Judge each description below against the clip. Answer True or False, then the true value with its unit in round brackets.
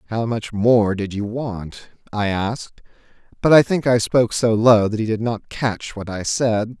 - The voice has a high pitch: False (110 Hz)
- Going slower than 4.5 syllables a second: True (4.3 syllables/s)